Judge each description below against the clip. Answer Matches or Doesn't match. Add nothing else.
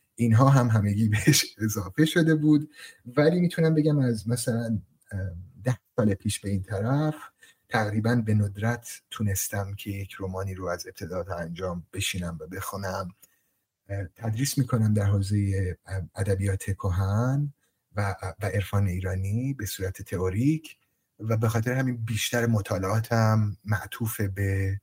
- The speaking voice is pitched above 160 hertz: Doesn't match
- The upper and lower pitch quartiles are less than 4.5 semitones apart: Matches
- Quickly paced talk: Doesn't match